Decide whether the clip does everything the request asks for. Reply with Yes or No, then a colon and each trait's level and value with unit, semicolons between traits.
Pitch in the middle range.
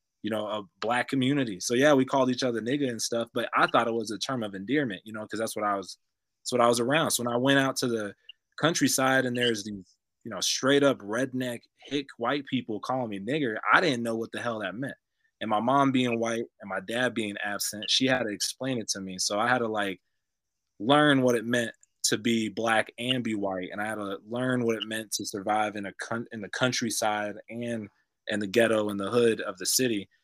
No: low, 115 Hz